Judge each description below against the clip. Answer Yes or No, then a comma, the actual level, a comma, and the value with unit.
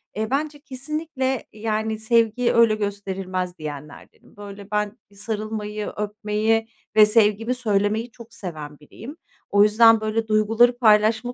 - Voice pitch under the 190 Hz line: No, high, 215 Hz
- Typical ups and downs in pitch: No, narrow, 2.0 semitones